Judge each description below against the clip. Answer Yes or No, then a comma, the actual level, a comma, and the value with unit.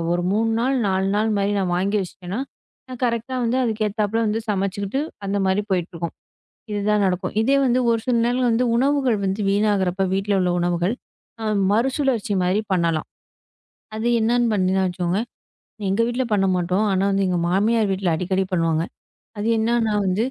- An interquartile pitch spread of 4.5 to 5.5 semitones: No, average, 3.5 semitones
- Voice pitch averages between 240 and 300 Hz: No, high, 205 Hz